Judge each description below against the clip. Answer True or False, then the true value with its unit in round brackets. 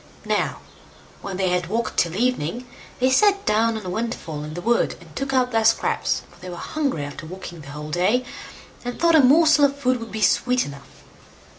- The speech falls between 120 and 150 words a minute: False (205 wpm)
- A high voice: True (225 Hz)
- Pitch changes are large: True (6.5 semitones)